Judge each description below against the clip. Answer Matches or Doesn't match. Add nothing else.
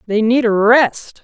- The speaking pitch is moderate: Doesn't match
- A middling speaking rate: Matches